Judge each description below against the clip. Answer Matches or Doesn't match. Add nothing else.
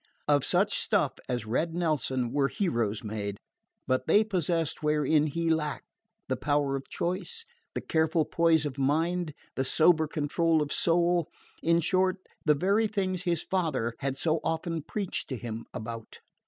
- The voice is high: Doesn't match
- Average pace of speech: Matches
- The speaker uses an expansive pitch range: Doesn't match